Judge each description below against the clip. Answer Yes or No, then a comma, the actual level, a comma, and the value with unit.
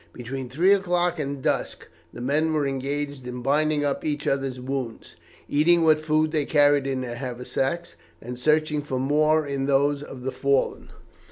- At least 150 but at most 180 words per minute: Yes, average, 170 wpm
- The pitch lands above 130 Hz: Yes, medium, 140 Hz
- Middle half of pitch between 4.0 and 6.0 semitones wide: No, narrow, 2.6 semitones